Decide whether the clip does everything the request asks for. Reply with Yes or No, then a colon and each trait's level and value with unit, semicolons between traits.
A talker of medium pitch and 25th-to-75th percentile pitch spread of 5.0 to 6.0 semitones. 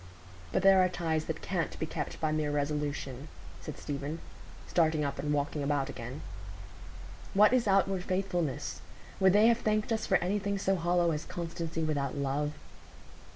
No: medium, 160 Hz; average, 4.6 semitones